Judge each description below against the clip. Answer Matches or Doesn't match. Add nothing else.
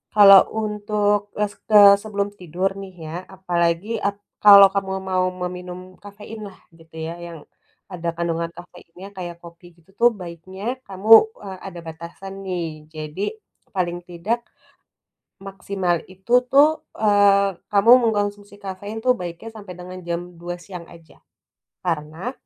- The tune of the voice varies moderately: Matches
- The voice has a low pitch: Doesn't match